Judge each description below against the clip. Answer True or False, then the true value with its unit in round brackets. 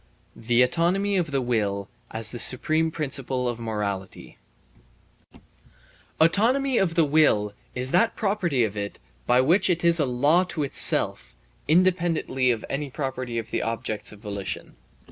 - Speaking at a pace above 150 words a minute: False (145 wpm)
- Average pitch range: False (6.6 semitones)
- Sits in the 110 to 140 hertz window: True (135 Hz)